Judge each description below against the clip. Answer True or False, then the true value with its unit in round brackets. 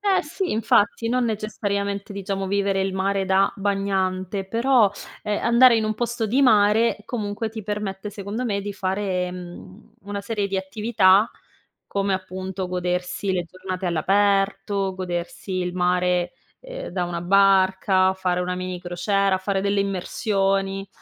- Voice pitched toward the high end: True (195 Hz)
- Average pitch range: False (1.8 semitones)